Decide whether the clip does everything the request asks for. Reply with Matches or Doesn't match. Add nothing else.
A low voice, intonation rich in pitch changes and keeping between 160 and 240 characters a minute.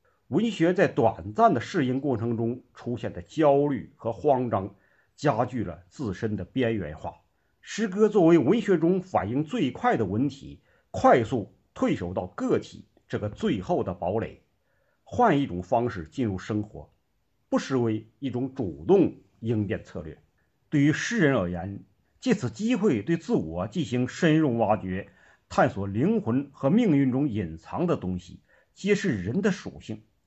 Matches